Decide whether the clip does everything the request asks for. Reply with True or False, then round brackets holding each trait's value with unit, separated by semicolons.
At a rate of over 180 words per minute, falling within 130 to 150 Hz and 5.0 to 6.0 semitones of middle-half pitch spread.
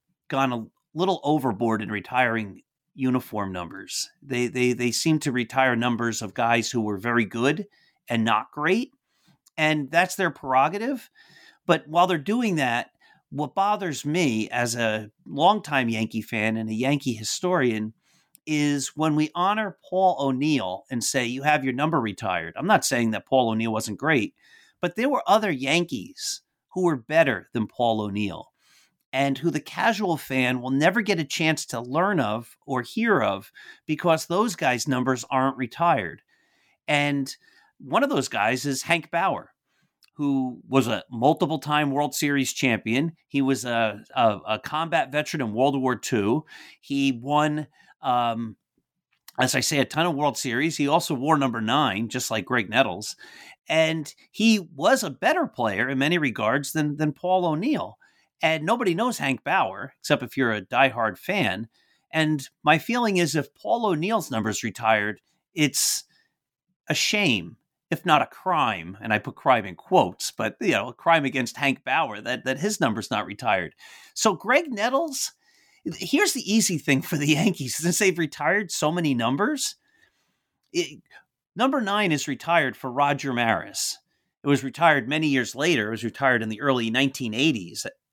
False (165 wpm; 140 Hz; 5.4 semitones)